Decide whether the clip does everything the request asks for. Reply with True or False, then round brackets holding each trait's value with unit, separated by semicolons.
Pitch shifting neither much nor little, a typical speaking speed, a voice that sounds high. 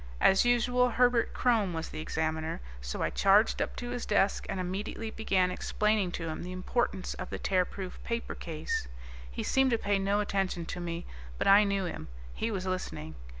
True (3.9 semitones; 190 wpm; 195 Hz)